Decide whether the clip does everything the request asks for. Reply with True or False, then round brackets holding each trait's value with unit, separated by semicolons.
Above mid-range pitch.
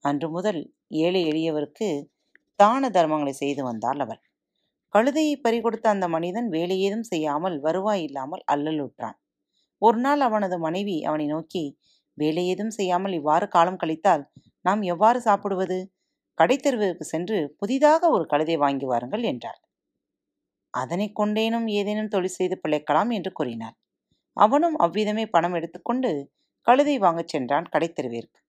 False (180 Hz)